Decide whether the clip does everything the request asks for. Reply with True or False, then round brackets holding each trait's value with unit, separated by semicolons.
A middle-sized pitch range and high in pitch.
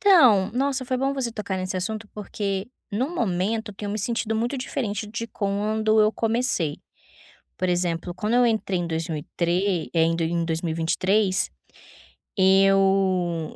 True (4.0 semitones; 200 Hz)